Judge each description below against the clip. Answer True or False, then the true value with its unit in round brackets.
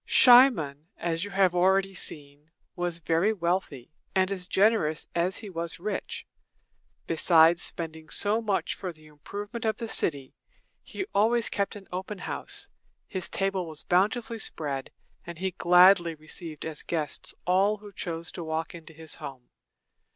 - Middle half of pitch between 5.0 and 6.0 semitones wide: False (3.7 semitones)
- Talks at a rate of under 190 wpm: True (150 wpm)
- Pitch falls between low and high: True (175 Hz)